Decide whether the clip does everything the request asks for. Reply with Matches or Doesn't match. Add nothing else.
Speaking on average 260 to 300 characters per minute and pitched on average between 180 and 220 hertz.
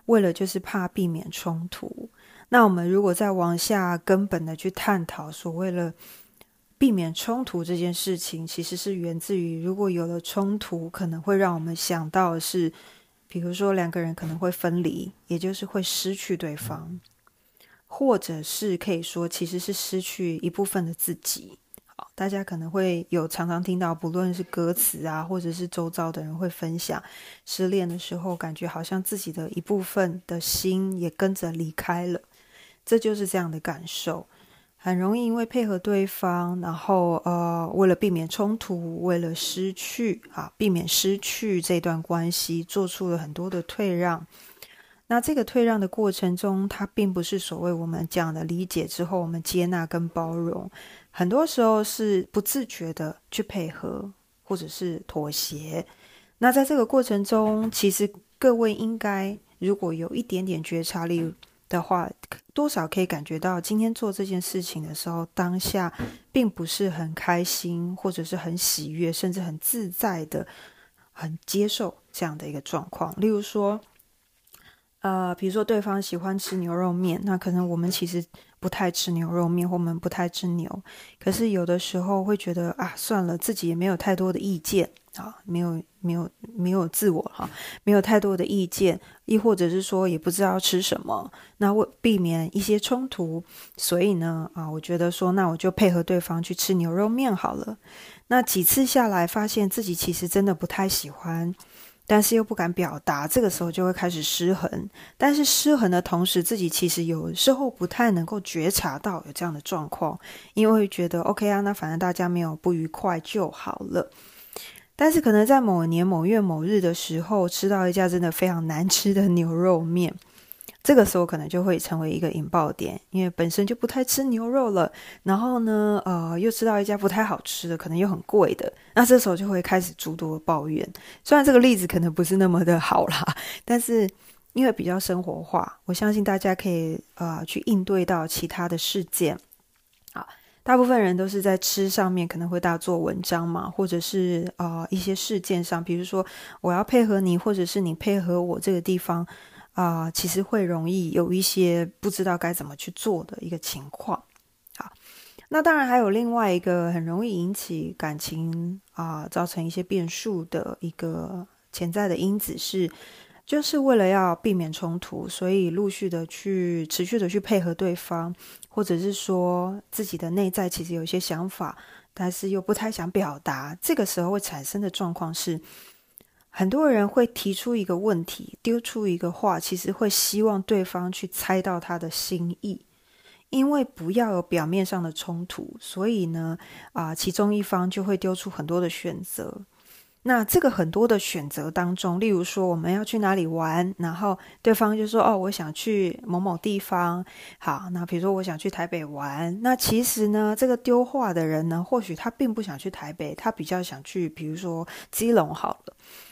Matches